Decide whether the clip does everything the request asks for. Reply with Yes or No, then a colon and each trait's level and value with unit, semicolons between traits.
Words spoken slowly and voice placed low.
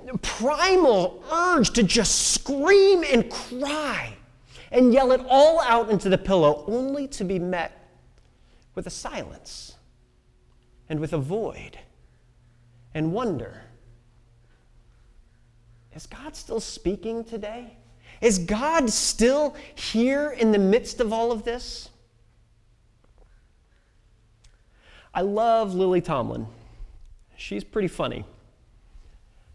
No: slow, 105 wpm; high, 190 Hz